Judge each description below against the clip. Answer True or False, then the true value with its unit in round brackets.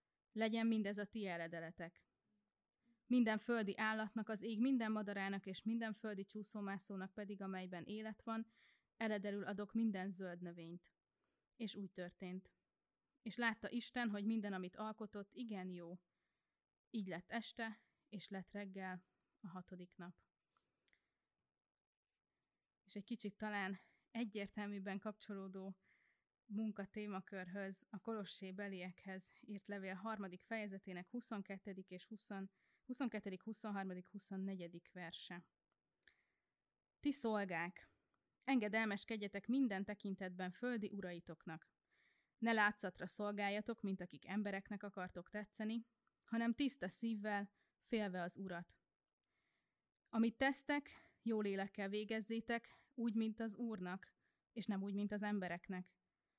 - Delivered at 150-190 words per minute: False (110 wpm)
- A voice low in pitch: False (205 Hz)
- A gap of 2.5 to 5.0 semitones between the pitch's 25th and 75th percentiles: True (2.8 semitones)